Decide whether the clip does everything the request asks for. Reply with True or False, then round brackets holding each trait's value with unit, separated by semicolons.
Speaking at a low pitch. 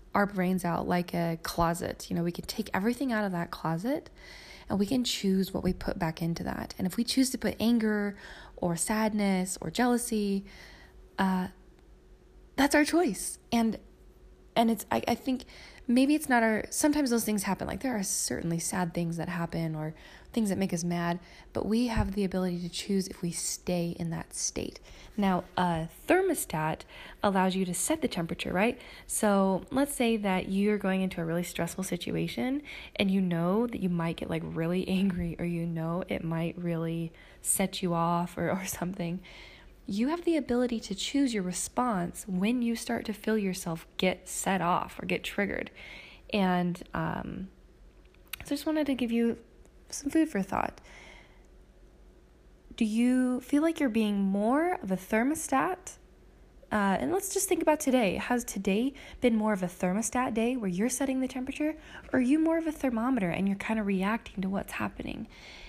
False (200 Hz)